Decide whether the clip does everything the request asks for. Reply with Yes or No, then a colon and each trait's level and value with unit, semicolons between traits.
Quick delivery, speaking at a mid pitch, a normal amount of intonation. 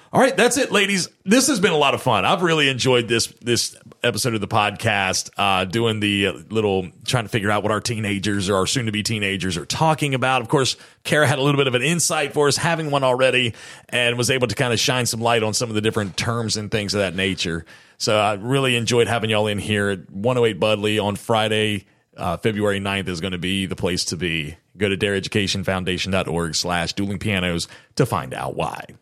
No: fast, 225 wpm; low, 110 Hz; average, 4.2 semitones